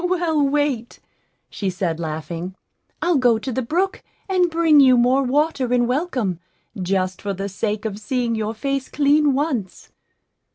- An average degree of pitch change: No, wide, 6.3 semitones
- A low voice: No, very high, 250 Hz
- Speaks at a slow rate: No, average, 155 wpm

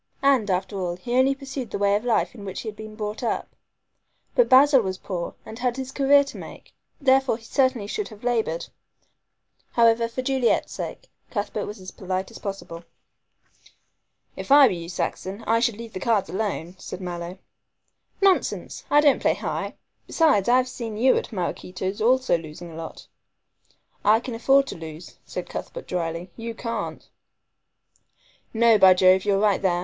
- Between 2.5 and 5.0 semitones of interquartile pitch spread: No, wide, 5.4 semitones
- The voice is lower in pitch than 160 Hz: No, high, 220 Hz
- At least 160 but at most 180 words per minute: Yes, average, 175 wpm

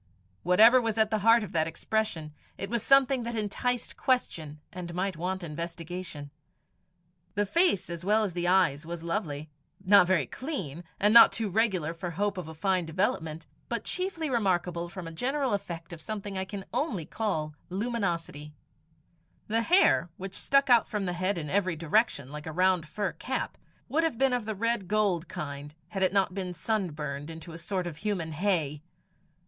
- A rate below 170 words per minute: No, average, 180 wpm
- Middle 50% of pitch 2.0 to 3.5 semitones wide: No, average, 4.8 semitones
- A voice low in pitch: No, medium, 185 Hz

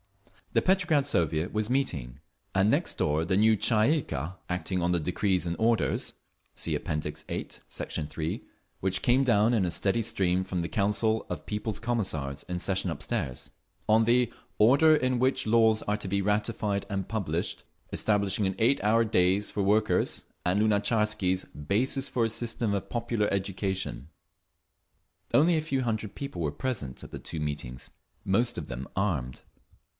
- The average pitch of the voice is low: Yes, low, 105 Hz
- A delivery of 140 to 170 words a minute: Yes, average, 165 wpm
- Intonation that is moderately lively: Yes, average, 4.4 semitones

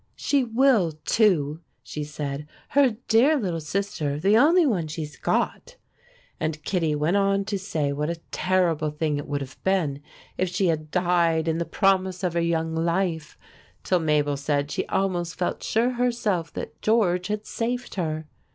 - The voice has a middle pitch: Yes, medium, 175 Hz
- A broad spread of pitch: No, average, 4.6 semitones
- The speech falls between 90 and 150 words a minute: No, average, 170 wpm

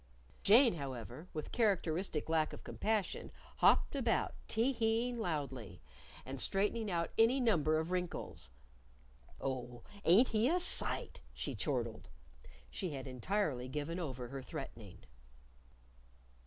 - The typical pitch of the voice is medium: Yes, medium, 170 Hz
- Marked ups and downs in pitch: Yes, wide, 8.6 semitones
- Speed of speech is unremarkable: No, slow, 120 wpm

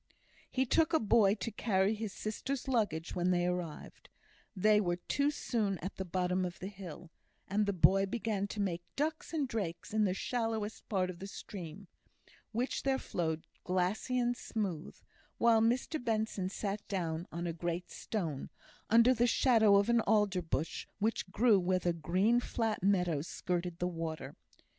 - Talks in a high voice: Yes, high, 200 Hz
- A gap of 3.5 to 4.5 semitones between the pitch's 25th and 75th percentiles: Yes, average, 4.1 semitones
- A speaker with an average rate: Yes, average, 170 wpm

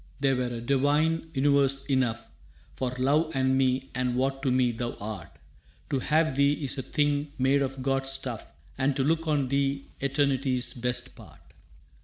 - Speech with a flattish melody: Yes, narrow, 1.7 semitones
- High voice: No, low, 135 Hz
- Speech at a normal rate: Yes, average, 170 wpm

